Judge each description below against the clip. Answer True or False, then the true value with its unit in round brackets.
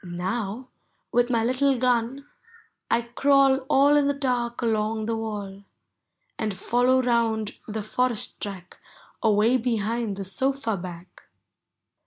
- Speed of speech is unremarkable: False (125 wpm)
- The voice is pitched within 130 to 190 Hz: False (230 Hz)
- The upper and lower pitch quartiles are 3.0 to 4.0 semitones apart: True (3.3 semitones)